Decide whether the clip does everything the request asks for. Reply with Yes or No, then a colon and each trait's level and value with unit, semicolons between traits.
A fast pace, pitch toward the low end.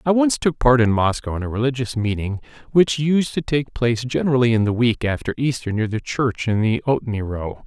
Yes: fast, 220 wpm; low, 125 Hz